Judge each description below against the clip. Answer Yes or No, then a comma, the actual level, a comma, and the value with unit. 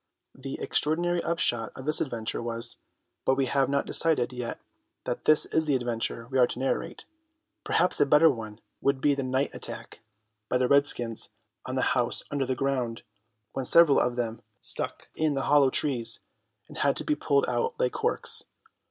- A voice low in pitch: Yes, low, 130 Hz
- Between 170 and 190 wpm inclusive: Yes, average, 180 wpm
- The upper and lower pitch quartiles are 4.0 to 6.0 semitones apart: No, average, 2.9 semitones